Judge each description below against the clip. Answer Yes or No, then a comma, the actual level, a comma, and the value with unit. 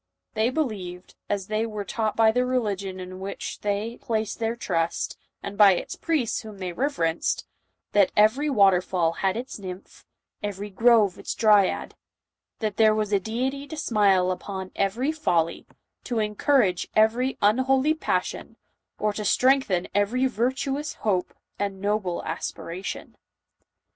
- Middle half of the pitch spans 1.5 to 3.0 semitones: No, average, 4.0 semitones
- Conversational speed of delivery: Yes, average, 150 wpm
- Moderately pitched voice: No, high, 210 Hz